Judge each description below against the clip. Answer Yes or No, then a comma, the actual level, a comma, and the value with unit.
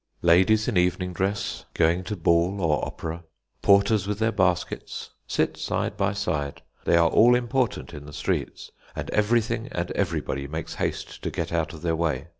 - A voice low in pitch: Yes, very low, 90 Hz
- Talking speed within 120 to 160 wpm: No, average, 175 wpm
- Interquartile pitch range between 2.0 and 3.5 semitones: No, average, 3.9 semitones